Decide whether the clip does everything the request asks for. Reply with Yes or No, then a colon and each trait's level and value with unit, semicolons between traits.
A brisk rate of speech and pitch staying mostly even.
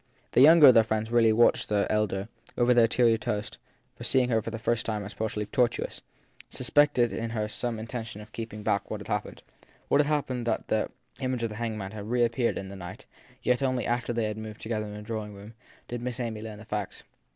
Yes: fast, 240 wpm; narrow, 2.2 semitones